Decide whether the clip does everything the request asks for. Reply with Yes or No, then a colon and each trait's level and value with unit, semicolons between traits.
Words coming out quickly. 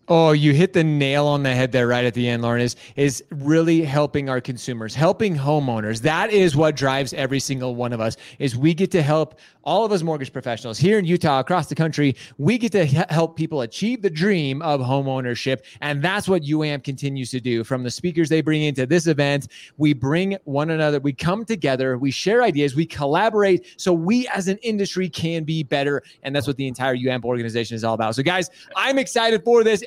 Yes: fast, 215 wpm